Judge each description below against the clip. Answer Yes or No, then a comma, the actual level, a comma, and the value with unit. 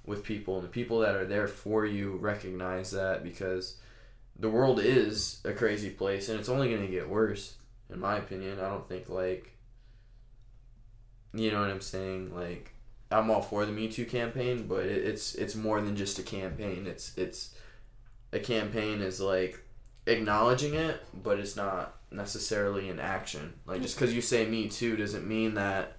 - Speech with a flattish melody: No, average, 3.1 semitones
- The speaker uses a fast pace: No, average, 180 wpm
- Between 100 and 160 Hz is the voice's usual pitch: Yes, low, 110 Hz